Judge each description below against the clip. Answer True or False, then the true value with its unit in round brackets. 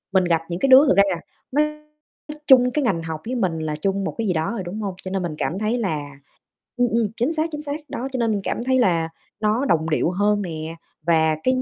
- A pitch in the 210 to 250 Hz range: False (200 Hz)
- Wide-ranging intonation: True (6.9 semitones)